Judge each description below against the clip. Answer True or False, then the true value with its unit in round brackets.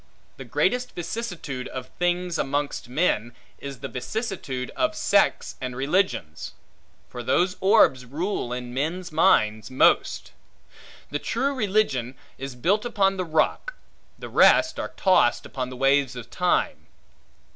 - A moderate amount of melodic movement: False (7.2 semitones)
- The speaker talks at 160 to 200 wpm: False (135 wpm)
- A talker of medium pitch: True (145 Hz)